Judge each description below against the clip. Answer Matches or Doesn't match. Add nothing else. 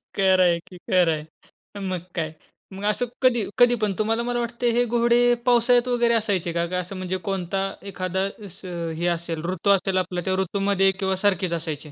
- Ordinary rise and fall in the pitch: Matches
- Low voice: Doesn't match